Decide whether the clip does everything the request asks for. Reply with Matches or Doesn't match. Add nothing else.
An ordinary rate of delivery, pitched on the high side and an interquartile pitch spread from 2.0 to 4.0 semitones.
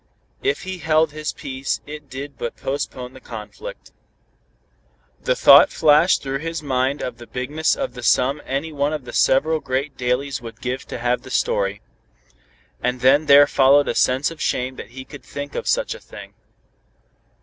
Doesn't match